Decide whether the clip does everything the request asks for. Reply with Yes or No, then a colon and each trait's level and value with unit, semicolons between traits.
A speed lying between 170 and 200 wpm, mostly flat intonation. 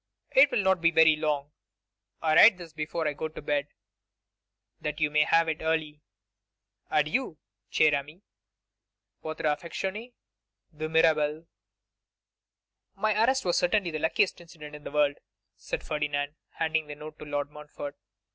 No: average, 145 wpm; narrow, 2.0 semitones